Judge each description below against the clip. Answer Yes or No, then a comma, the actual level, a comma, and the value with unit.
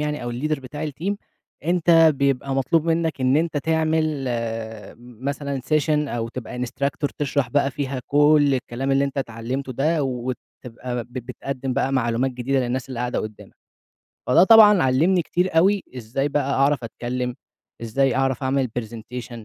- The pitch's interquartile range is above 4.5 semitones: No, average, 3.2 semitones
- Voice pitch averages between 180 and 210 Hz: No, low, 135 Hz